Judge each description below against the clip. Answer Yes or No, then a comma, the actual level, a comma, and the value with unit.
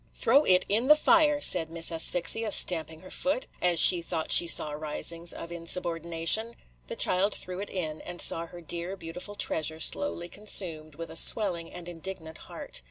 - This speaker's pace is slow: No, average, 175 wpm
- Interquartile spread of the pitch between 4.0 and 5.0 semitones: No, average, 3.2 semitones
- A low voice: No, medium, 175 Hz